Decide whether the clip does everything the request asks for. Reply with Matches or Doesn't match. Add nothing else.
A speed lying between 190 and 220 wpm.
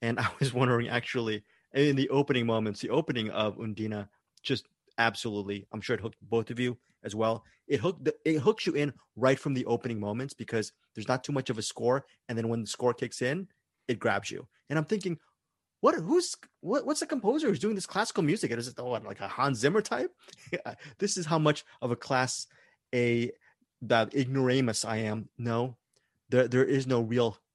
Matches